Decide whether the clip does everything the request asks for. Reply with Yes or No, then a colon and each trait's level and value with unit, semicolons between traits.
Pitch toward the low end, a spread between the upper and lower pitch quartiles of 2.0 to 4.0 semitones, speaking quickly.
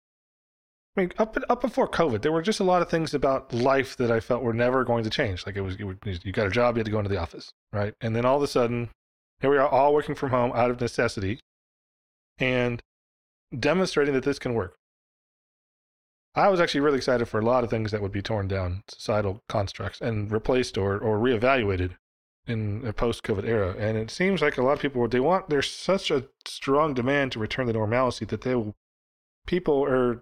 No: low, 120 Hz; average, 4.9 semitones; fast, 220 wpm